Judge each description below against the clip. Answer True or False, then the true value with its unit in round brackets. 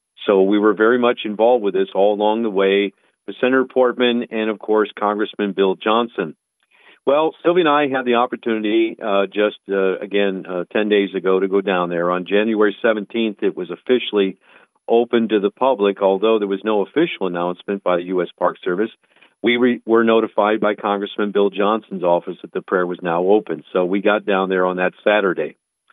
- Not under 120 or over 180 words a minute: False (195 wpm)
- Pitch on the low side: True (105 Hz)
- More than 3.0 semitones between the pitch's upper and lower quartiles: False (2.7 semitones)